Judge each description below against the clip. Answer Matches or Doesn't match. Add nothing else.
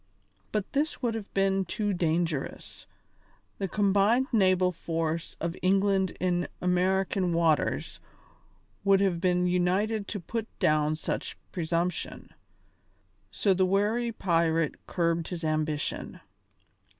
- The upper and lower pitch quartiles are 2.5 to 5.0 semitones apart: Matches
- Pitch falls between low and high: Matches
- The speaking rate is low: Matches